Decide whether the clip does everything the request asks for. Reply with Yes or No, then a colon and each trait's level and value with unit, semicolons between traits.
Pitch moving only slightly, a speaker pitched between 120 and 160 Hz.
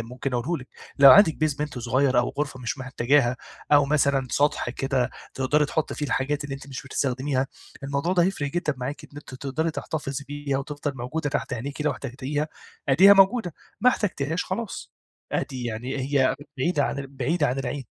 Yes: narrow, 2.3 semitones; medium, 140 Hz